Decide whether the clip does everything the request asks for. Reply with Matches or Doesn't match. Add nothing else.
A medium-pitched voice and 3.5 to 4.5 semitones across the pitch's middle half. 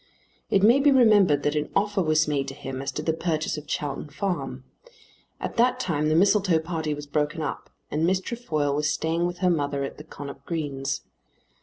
Matches